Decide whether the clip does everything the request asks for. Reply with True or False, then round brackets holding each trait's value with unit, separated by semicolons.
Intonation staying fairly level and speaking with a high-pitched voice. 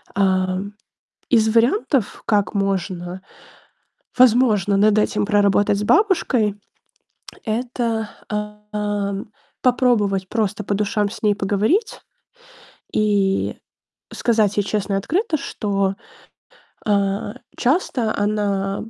True (2.2 semitones; 210 Hz)